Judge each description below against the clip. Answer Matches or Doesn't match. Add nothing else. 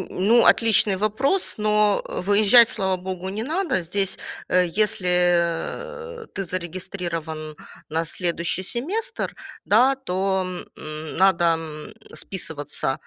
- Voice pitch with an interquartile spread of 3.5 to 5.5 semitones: Matches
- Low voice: Doesn't match